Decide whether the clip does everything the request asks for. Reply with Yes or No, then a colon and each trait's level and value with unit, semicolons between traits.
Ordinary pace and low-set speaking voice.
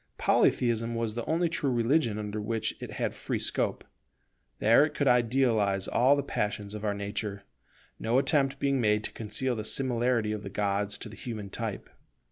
Yes: average, 175 wpm; low, 115 Hz